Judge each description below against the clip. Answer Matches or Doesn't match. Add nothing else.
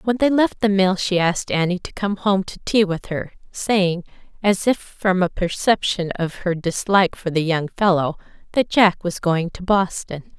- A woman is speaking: Matches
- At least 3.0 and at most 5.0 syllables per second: Matches